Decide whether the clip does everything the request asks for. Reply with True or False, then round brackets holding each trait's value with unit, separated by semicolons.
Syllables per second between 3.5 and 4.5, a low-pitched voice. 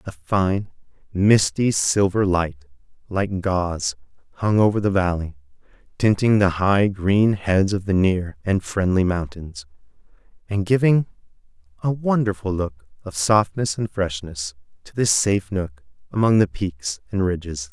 True (4.2 syllables/s; 95 Hz)